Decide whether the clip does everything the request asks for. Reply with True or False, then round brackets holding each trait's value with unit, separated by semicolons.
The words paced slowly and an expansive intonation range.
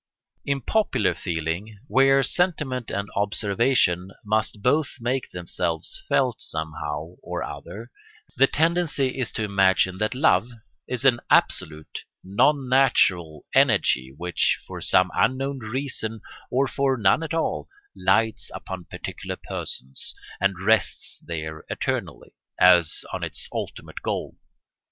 True (125 wpm; 6.9 semitones)